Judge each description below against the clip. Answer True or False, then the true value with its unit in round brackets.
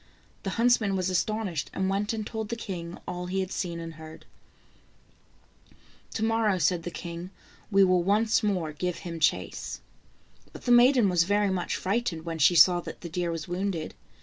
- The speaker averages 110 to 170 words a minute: False (180 wpm)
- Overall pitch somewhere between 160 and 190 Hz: True (185 Hz)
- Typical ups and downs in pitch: True (3.4 semitones)